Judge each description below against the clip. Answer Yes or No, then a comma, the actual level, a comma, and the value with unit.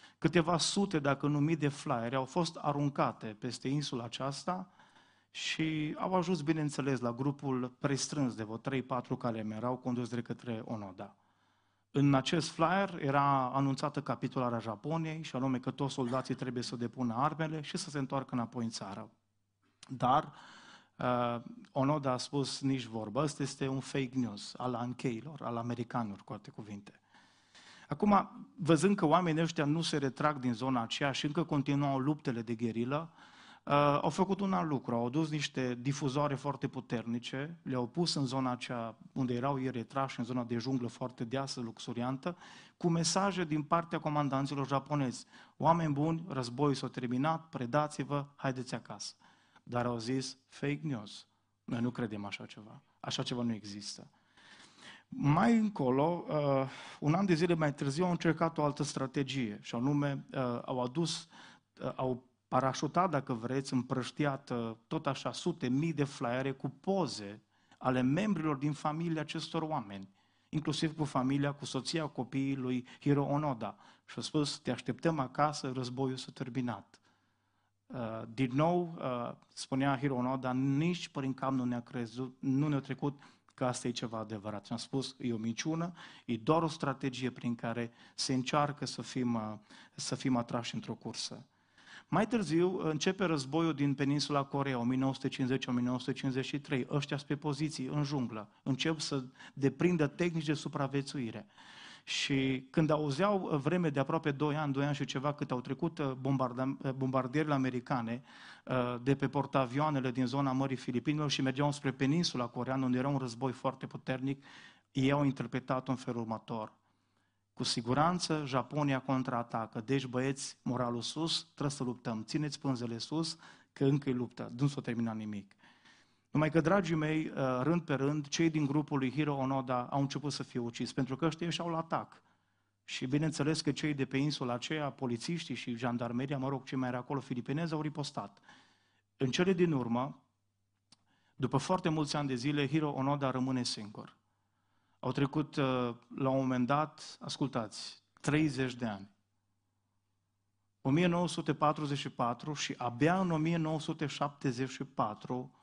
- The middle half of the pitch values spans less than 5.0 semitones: Yes, average, 3.4 semitones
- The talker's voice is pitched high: No, low, 135 Hz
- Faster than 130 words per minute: Yes, average, 150 wpm